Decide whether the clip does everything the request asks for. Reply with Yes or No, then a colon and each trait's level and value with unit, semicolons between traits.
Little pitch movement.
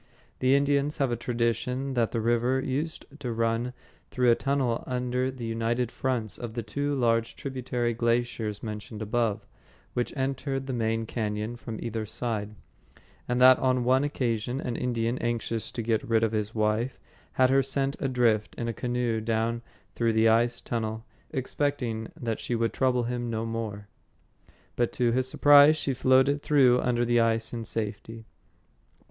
Yes: narrow, 2.3 semitones